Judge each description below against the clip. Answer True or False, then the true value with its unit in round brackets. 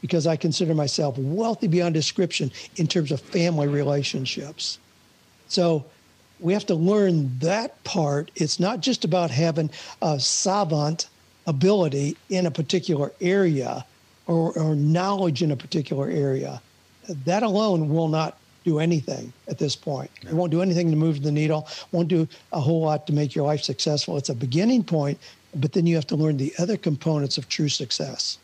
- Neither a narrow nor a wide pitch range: True (3.2 semitones)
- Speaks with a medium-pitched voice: True (160 Hz)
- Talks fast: False (170 wpm)